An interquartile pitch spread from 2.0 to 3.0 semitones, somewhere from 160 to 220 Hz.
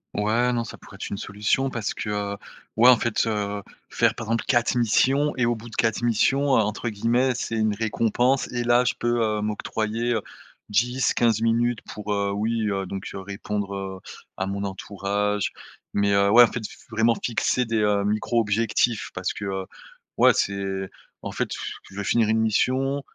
No: average, 2.7 semitones; low, 110 Hz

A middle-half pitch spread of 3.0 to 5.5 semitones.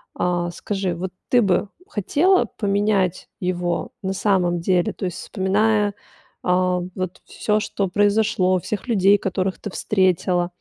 No: narrow, 2.4 semitones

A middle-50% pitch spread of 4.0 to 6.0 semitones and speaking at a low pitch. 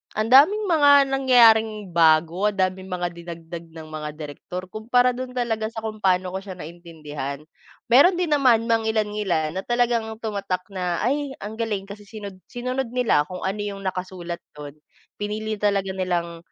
No: average, 4.7 semitones; high, 205 Hz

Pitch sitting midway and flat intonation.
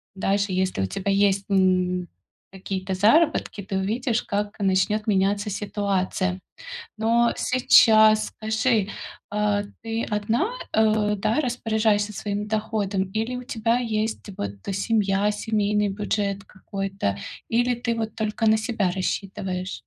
No: high, 210 Hz; narrow, 2.1 semitones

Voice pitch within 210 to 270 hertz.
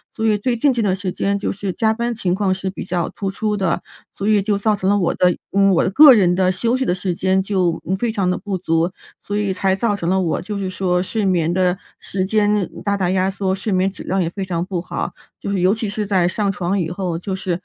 No: high, 190 Hz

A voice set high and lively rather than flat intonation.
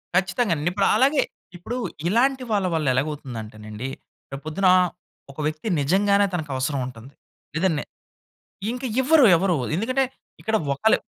No: medium, 180 Hz; wide, 7.8 semitones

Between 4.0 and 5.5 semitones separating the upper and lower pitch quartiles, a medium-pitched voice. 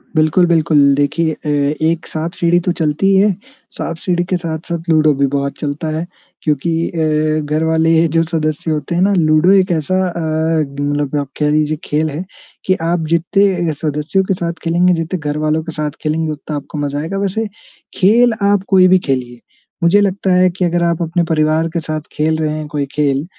No: narrow, 2.4 semitones; medium, 160 Hz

